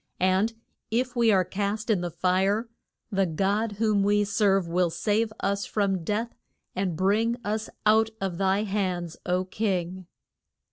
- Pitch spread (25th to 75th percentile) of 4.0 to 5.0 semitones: No, narrow, 2.5 semitones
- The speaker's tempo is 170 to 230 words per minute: No, average, 150 wpm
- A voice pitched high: Yes, high, 200 Hz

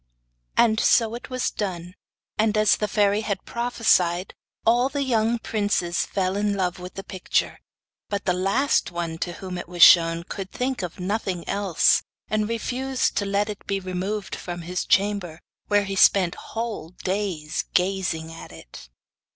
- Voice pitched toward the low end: No, high, 195 Hz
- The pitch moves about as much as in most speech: Yes, average, 3.2 semitones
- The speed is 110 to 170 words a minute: Yes, average, 165 wpm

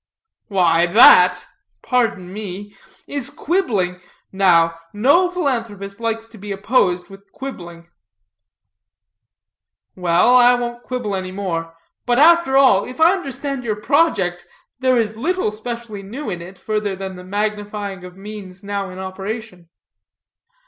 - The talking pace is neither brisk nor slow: No, slow, 130 wpm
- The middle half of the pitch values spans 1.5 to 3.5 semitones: No, average, 4.8 semitones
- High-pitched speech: Yes, high, 205 Hz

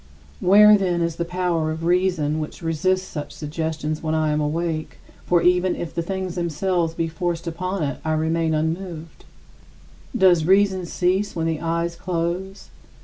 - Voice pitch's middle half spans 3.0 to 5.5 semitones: No, narrow, 2.4 semitones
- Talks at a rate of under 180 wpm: Yes, average, 160 wpm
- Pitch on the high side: No, medium, 170 Hz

